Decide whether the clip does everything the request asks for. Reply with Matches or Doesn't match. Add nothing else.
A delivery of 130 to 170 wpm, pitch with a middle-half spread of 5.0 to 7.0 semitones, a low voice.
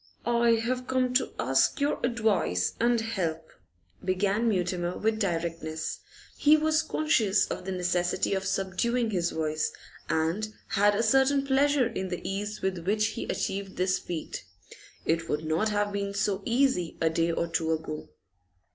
Doesn't match